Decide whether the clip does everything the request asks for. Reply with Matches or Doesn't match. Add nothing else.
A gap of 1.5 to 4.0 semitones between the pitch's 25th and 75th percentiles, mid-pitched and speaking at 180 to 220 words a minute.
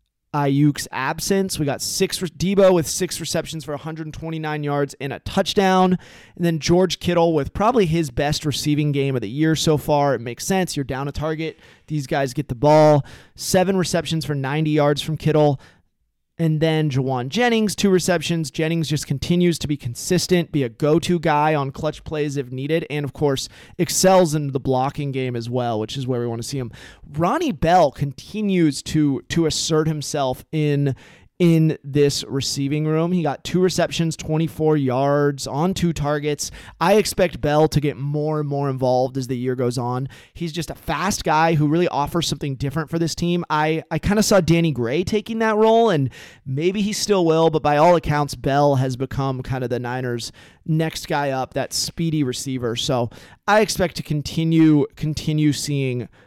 Matches